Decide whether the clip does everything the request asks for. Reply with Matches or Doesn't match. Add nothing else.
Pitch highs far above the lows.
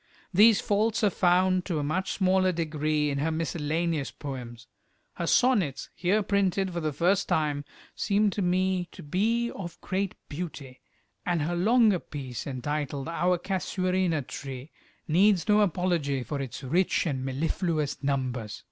Doesn't match